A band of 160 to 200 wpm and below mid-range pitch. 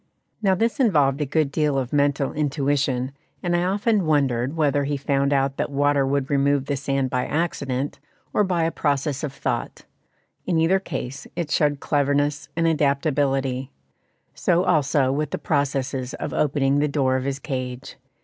No: average, 170 wpm; medium, 145 Hz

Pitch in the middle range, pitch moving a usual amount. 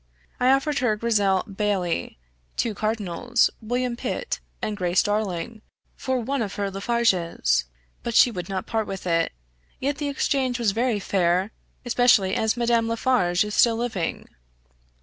No: high, 220 Hz; average, 3.9 semitones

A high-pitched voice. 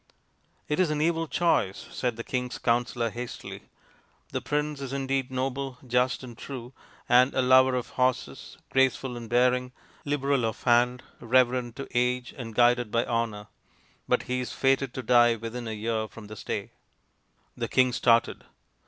No: low, 125 Hz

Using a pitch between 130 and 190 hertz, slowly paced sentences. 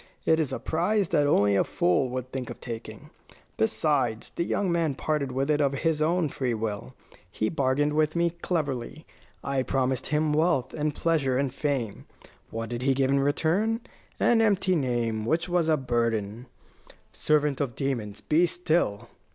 No: medium, 140 Hz; average, 175 wpm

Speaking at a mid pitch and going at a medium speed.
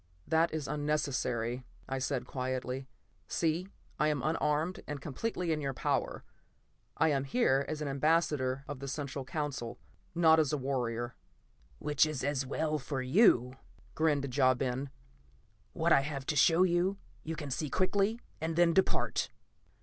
Yes: medium, 145 Hz; average, 155 wpm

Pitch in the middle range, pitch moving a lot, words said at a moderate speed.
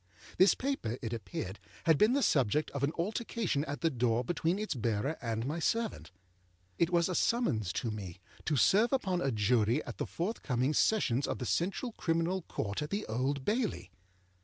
Yes: medium, 150 Hz; wide, 8.2 semitones; average, 185 wpm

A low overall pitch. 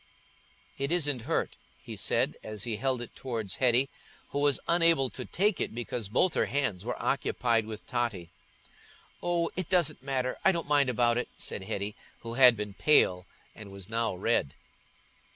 Yes: low, 125 Hz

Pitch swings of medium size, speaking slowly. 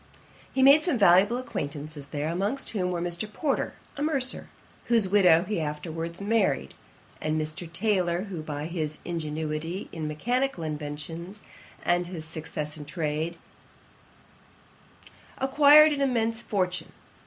No: wide, 6.1 semitones; slow, 130 wpm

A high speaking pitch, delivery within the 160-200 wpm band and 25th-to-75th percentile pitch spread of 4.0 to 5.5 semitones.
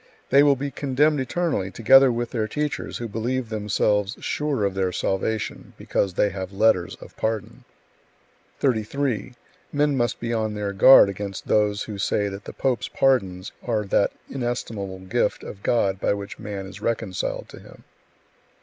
No: low, 110 Hz; average, 165 wpm; average, 4.3 semitones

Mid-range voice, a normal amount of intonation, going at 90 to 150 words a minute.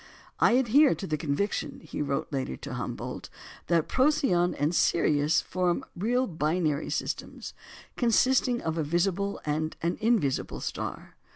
No: medium, 175 Hz; wide, 7.0 semitones; slow, 135 wpm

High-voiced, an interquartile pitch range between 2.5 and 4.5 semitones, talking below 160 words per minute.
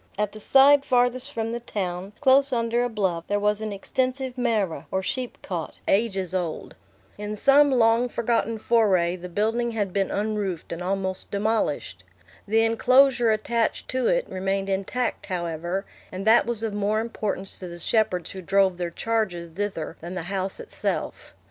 No: high, 210 Hz; average, 3.9 semitones; average, 165 wpm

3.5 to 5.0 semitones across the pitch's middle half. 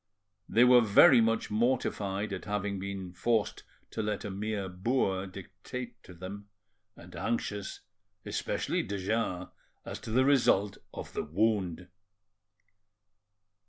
No: average, 3.0 semitones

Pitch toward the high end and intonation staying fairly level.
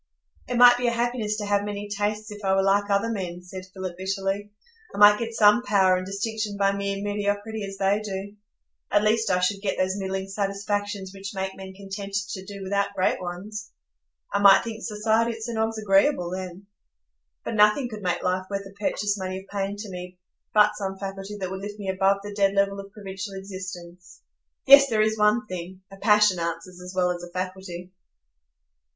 Yes: high, 200 Hz; narrow, 1.6 semitones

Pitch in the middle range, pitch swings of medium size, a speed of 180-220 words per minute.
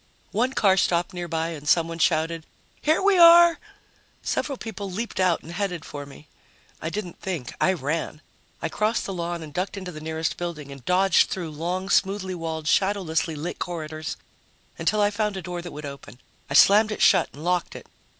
Yes: medium, 175 Hz; average, 3.7 semitones; average, 190 wpm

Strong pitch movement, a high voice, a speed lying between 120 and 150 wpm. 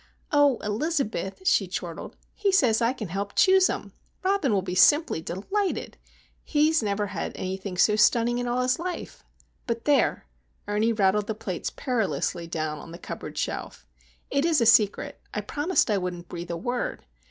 No: wide, 7.0 semitones; high, 220 Hz; average, 170 wpm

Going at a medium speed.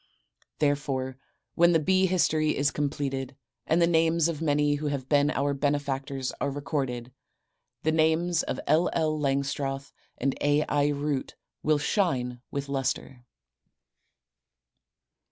No: slow, 130 wpm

